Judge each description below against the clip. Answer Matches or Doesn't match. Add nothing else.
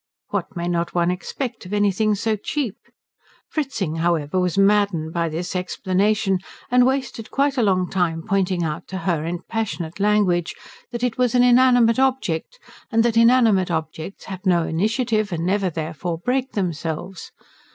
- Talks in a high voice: Matches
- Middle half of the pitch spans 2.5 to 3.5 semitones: Doesn't match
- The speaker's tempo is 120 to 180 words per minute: Matches